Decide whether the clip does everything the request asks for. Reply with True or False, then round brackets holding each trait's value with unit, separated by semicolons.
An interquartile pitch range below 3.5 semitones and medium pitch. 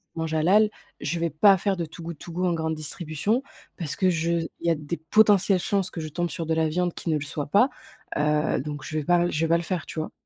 True (2.5 semitones; 165 Hz)